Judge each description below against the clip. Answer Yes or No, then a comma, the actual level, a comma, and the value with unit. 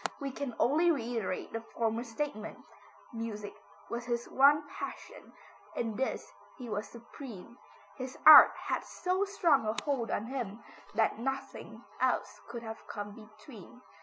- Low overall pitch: No, high, 235 Hz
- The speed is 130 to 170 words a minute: Yes, slow, 135 wpm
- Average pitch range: Yes, average, 3.7 semitones